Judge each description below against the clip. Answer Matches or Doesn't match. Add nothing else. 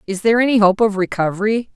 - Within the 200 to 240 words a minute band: Matches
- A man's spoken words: Doesn't match